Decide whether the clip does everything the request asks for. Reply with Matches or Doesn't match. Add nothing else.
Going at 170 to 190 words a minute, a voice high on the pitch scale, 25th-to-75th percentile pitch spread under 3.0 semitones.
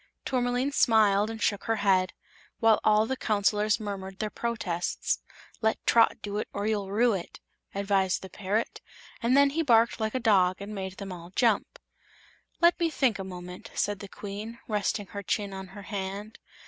Matches